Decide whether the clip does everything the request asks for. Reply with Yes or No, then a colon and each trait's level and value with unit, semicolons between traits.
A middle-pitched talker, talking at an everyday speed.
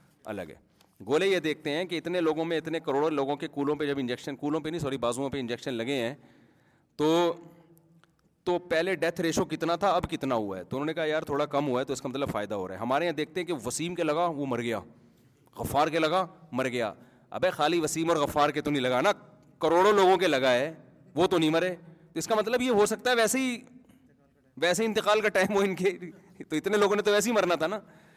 No: medium, 165 Hz; fast, 250 wpm